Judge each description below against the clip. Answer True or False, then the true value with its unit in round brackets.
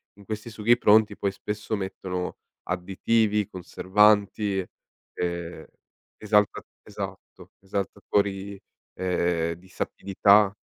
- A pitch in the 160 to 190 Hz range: False (100 Hz)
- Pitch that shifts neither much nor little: False (2.0 semitones)